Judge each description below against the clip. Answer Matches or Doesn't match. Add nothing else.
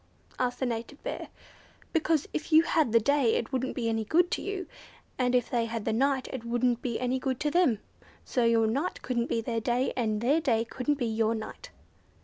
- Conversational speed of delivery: Doesn't match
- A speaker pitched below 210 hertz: Doesn't match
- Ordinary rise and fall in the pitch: Matches